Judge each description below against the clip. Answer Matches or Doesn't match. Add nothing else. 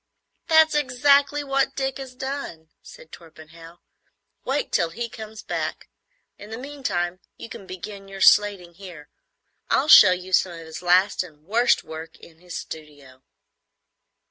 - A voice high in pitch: Matches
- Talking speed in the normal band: Matches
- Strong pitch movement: Matches